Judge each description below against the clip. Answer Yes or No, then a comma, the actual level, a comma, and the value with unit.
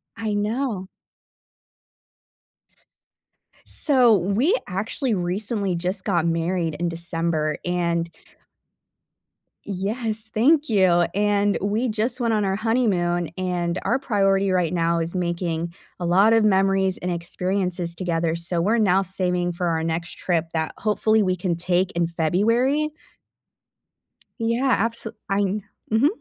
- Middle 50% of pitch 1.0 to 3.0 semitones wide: No, average, 3.9 semitones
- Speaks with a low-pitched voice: No, high, 190 Hz